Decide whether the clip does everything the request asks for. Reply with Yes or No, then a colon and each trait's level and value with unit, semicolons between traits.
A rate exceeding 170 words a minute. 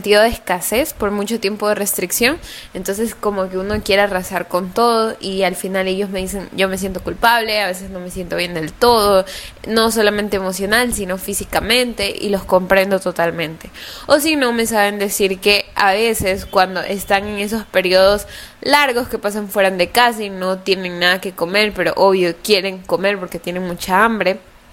Yes: average, 185 wpm